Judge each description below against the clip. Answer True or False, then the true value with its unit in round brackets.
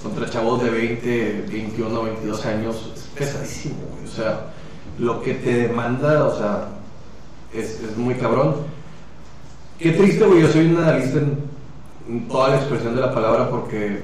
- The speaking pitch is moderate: False (120 Hz)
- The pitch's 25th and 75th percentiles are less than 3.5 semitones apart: False (3.9 semitones)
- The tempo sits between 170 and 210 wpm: False (160 wpm)